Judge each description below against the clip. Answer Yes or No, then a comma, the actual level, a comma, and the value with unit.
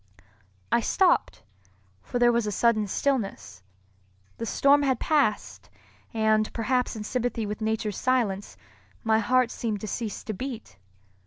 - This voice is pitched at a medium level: No, high, 230 Hz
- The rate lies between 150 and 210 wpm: No, average, 140 wpm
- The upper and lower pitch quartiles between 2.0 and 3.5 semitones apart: Yes, average, 2.9 semitones